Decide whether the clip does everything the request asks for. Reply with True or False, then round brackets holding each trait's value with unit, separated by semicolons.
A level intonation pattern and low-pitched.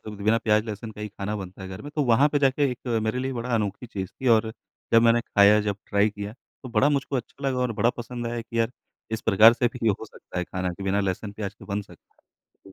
False (3.1 semitones; 110 Hz)